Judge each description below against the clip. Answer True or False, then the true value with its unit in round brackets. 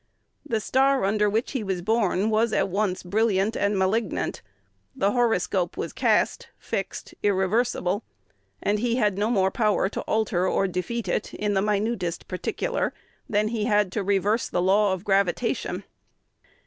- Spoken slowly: False (155 wpm)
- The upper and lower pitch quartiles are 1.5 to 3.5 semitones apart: True (2.7 semitones)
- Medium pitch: False (205 Hz)